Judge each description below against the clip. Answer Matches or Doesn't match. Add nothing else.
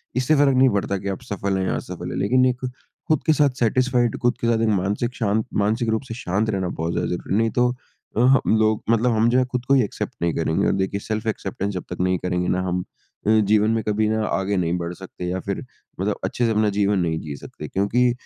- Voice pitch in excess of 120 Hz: Doesn't match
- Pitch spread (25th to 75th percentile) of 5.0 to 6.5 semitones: Doesn't match